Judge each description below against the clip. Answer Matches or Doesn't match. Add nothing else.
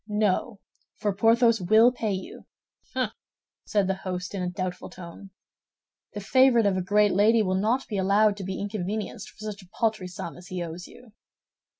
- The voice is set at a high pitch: Matches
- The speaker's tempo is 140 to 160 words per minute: Doesn't match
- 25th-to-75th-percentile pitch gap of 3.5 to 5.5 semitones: Doesn't match